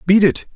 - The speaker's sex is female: No, male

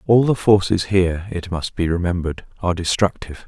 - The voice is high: No, very low, 90 Hz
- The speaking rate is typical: Yes, average, 175 wpm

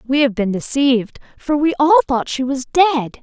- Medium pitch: No, very high, 260 Hz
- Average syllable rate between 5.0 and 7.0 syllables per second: Yes, 5.3 syllables/s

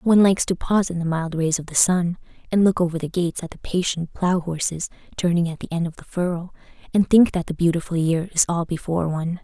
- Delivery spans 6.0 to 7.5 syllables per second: Yes, 6.2 syllables/s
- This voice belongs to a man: No, female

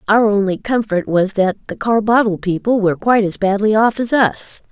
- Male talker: No, female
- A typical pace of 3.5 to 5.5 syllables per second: Yes, 5.3 syllables/s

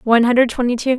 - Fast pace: Yes, fast, 245 wpm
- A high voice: Yes, high, 245 Hz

